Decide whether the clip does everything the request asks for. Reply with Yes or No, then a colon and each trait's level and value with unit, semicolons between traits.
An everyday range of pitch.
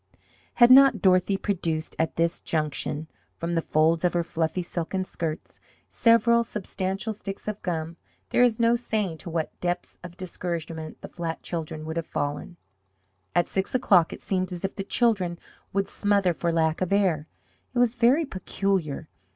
Yes: average, 3.8 semitones